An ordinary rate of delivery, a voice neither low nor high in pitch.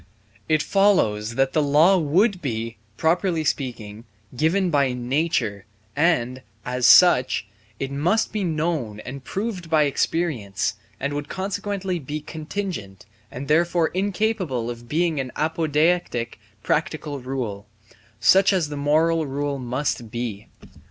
No: slow, 125 wpm; medium, 150 Hz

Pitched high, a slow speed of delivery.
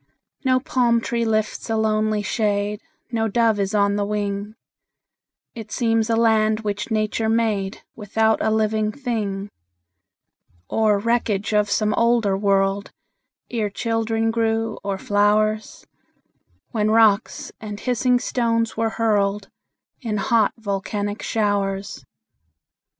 Yes: high, 215 Hz; slow, 120 wpm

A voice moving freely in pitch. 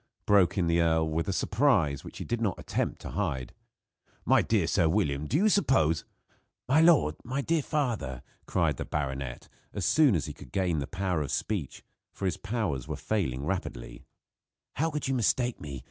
Yes: wide, 8.3 semitones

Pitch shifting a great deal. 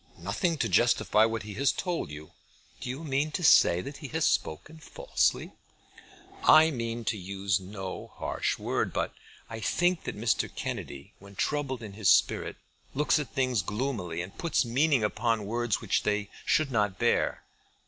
Yes: wide, 6.3 semitones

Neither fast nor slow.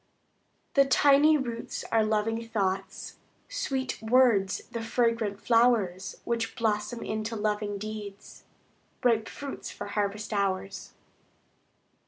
No: slow, 105 wpm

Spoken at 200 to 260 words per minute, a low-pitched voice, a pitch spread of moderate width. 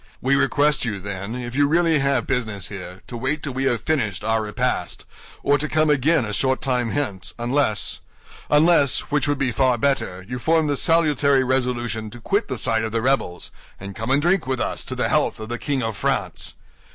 Yes: fast, 205 wpm; low, 130 Hz; average, 4.4 semitones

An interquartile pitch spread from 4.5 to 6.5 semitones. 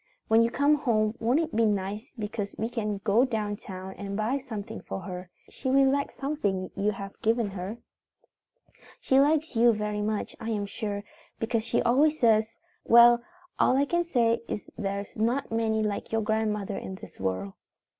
No: average, 3.0 semitones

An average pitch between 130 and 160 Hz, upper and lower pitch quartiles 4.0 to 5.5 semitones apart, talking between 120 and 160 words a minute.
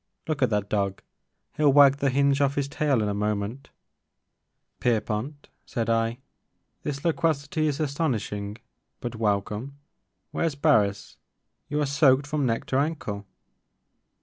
Yes: low, 135 Hz; average, 5.2 semitones; average, 150 wpm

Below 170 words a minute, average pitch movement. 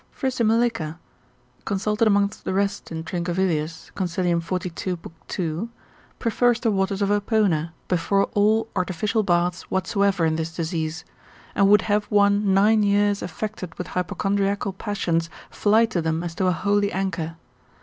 Yes: average, 140 wpm; average, 3.2 semitones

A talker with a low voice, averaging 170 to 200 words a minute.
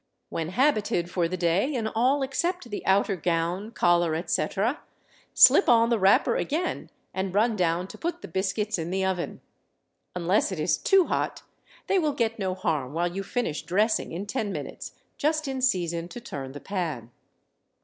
No: high, 190 Hz; average, 175 wpm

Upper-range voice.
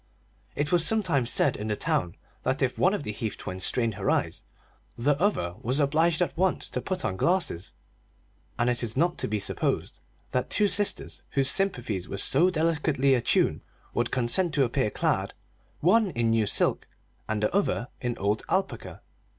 No: low, 135 Hz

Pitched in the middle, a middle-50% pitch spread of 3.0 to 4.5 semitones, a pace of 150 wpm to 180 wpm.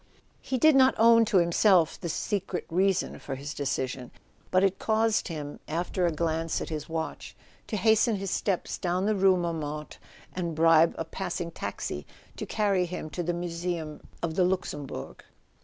Yes: medium, 175 Hz; average, 3.4 semitones; average, 170 wpm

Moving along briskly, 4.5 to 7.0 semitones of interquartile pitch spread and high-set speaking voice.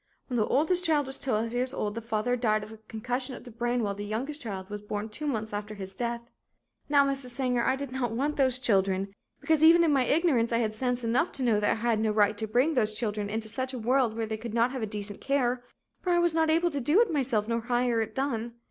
No: fast, 255 wpm; average, 3.8 semitones; high, 240 Hz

